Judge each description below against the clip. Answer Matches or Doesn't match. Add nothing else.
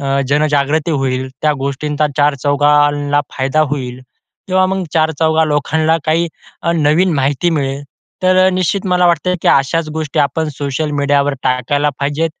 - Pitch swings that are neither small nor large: Doesn't match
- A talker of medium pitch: Matches